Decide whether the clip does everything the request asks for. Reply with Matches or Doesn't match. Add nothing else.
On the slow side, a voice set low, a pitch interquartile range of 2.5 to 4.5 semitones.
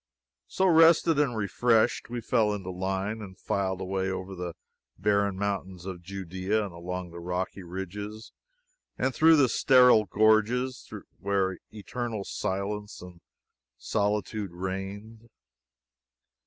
Matches